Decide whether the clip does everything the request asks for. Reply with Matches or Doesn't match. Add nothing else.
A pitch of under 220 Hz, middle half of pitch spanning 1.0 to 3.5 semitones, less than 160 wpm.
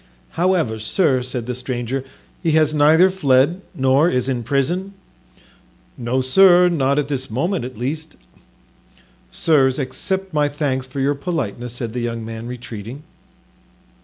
Doesn't match